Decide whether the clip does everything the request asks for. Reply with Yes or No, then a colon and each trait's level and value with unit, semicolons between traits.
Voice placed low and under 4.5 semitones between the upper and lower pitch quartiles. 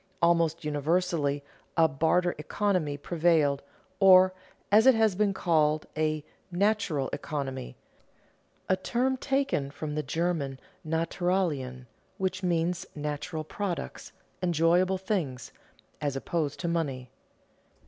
No: medium, 165 Hz; average, 4.0 semitones